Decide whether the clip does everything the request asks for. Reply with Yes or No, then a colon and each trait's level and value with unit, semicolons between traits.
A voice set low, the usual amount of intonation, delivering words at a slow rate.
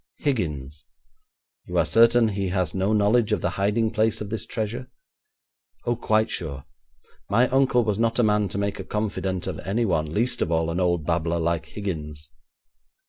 No: low, 100 Hz; average, 4.9 semitones; average, 175 wpm